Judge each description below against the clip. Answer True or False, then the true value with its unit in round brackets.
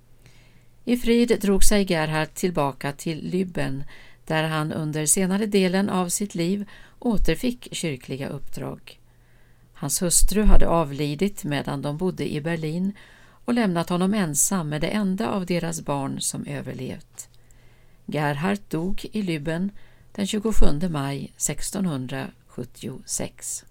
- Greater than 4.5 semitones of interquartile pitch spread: True (5.2 semitones)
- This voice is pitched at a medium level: True (170 Hz)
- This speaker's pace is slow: True (120 wpm)